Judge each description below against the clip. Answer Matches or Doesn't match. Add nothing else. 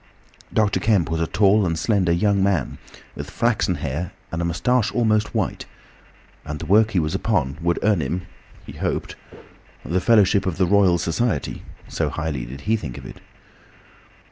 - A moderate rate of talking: Matches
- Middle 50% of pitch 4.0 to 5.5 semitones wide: Matches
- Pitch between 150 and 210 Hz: Doesn't match